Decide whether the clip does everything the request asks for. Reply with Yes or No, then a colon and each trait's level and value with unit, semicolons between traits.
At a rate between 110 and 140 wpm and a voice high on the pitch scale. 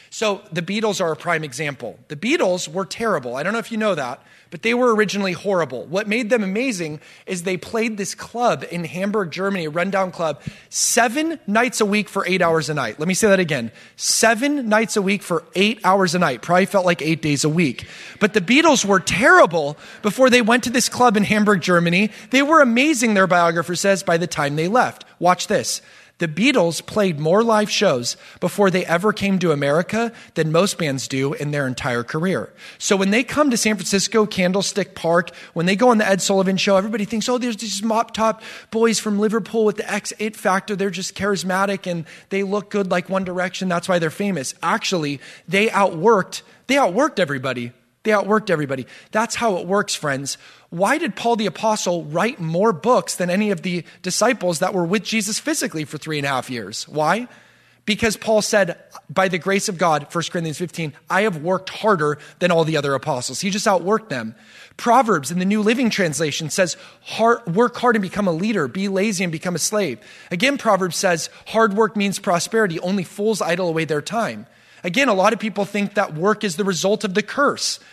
No: fast, 205 wpm; high, 195 Hz